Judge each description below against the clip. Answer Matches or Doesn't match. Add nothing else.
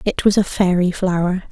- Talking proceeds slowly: Doesn't match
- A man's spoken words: Doesn't match